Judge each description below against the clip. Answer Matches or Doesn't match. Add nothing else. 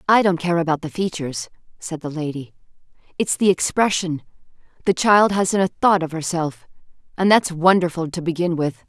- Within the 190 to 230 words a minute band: Doesn't match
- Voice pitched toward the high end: Doesn't match